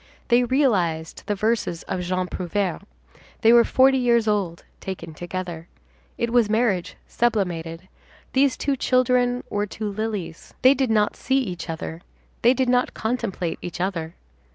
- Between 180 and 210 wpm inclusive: No, average, 150 wpm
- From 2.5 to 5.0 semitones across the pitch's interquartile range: No, wide, 5.6 semitones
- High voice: Yes, high, 210 Hz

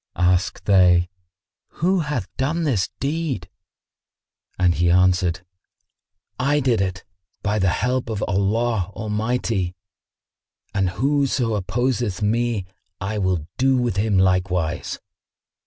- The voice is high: No, low, 105 Hz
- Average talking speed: No, slow, 110 wpm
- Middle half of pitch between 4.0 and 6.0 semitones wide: Yes, average, 5.2 semitones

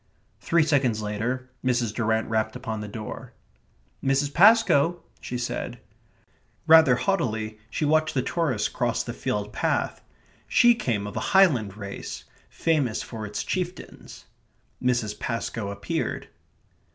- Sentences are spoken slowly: Yes, slow, 125 wpm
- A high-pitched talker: No, low, 125 Hz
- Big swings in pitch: Yes, wide, 6.5 semitones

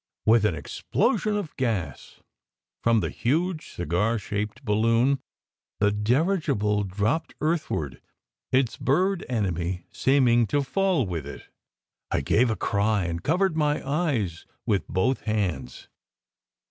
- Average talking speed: No, slow, 120 wpm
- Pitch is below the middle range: Yes, low, 115 Hz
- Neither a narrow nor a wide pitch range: No, wide, 6.5 semitones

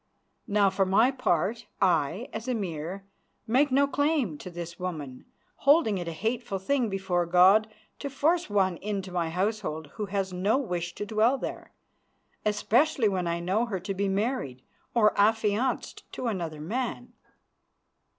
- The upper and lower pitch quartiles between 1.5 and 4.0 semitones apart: No, average, 4.7 semitones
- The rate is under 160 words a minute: Yes, average, 150 wpm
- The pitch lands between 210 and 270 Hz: No, high, 200 Hz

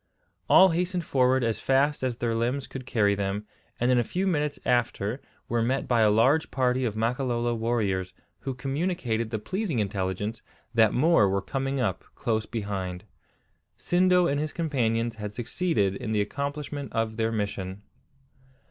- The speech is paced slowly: No, average, 160 wpm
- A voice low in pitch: Yes, low, 120 Hz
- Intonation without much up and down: No, average, 4.5 semitones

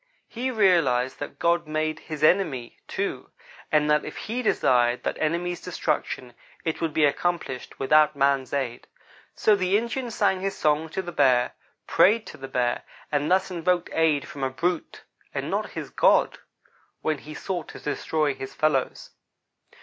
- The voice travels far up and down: No, average, 4.6 semitones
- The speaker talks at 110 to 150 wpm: No, average, 165 wpm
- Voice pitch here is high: No, medium, 155 Hz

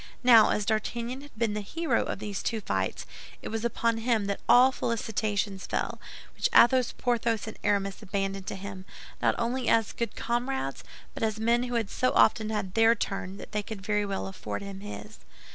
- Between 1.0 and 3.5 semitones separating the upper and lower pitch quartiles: Yes, average, 2.8 semitones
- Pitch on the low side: No, high, 220 Hz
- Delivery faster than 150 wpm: Yes, average, 195 wpm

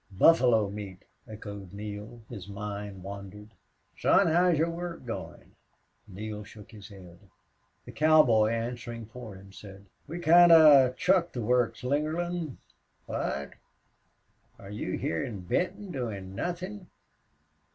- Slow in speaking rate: Yes, slow, 125 wpm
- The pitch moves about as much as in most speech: No, wide, 7.6 semitones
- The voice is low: Yes, low, 115 Hz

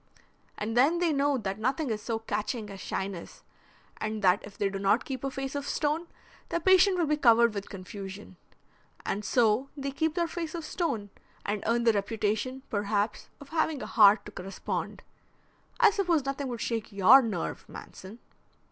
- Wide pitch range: Yes, wide, 5.8 semitones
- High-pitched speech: Yes, high, 235 Hz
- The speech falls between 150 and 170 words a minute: No, average, 180 wpm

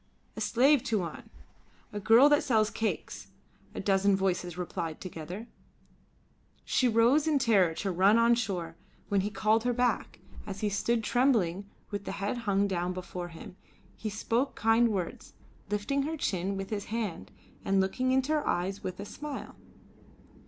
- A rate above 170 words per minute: No, average, 160 wpm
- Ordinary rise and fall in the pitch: Yes, average, 3.8 semitones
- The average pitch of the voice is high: Yes, high, 205 Hz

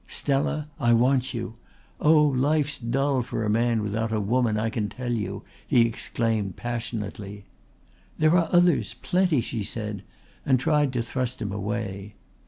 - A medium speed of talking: Yes, average, 155 wpm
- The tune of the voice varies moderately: Yes, average, 4.3 semitones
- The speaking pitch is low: Yes, low, 120 Hz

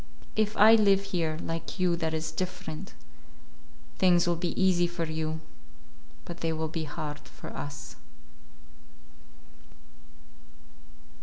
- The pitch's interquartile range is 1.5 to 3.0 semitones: Yes, narrow, 2.6 semitones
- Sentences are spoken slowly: Yes, slow, 120 wpm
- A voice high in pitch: No, medium, 170 Hz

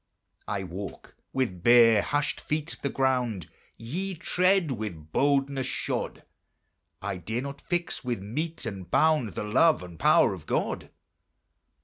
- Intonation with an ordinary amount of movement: No, wide, 6.7 semitones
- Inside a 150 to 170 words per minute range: No, slow, 135 wpm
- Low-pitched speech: Yes, low, 125 Hz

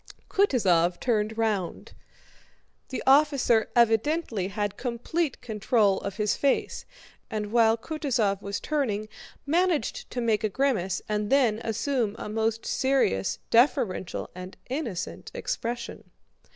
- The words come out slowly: Yes, slow, 115 wpm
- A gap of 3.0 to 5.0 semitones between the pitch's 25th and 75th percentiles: Yes, average, 4.3 semitones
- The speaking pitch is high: Yes, high, 225 Hz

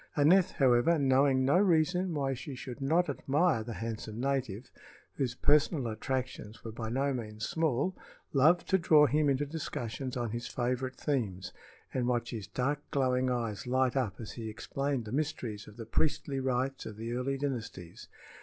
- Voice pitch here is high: No, low, 130 Hz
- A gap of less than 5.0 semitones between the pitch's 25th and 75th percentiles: Yes, average, 3.5 semitones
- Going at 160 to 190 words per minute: Yes, average, 170 wpm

